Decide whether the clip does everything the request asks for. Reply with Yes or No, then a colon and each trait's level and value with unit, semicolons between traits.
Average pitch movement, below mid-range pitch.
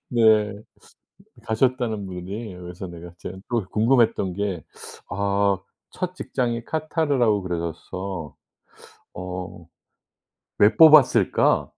Yes: average, 4.5 semitones; low, 100 Hz